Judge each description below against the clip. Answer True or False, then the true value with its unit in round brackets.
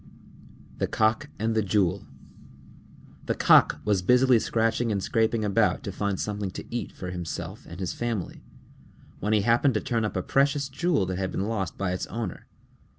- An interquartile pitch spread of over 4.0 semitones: False (3.6 semitones)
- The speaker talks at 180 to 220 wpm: True (185 wpm)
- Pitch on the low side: True (105 Hz)